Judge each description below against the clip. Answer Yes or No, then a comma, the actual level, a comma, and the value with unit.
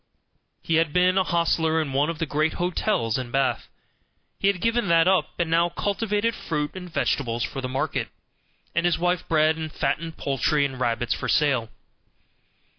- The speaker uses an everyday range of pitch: Yes, average, 4.0 semitones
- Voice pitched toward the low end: No, medium, 160 Hz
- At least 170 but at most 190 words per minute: Yes, average, 180 wpm